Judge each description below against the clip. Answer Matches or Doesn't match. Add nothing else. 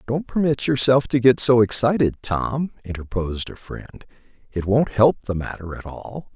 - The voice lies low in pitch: Matches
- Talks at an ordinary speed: Matches